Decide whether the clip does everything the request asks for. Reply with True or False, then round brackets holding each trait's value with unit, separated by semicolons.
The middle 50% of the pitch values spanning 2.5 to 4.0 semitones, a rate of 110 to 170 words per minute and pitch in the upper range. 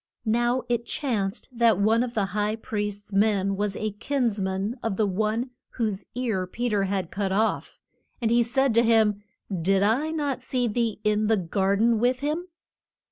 False (3.1 semitones; 185 wpm; 220 Hz)